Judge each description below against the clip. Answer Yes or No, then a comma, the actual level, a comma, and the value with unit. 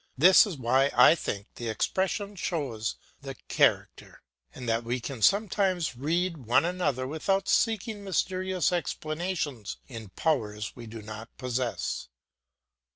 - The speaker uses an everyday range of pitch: No, wide, 7.8 semitones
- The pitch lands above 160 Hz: No, medium, 145 Hz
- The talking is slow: Yes, slow, 130 wpm